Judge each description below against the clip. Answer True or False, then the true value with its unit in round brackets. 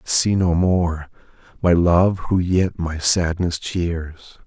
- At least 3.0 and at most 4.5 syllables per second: True (3.2 syllables/s)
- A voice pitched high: False (85 Hz)